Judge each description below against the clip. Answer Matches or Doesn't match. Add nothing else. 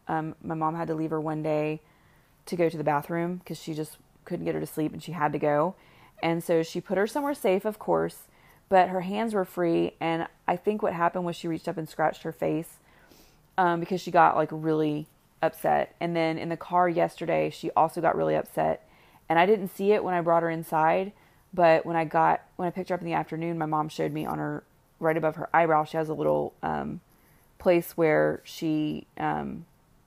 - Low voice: Doesn't match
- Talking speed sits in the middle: Doesn't match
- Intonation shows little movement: Matches